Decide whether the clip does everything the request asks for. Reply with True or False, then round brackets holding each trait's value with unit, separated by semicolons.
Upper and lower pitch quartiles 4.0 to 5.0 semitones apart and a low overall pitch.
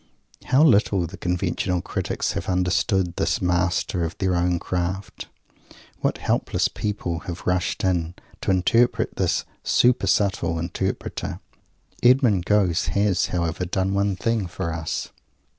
False (2.4 semitones; 90 Hz)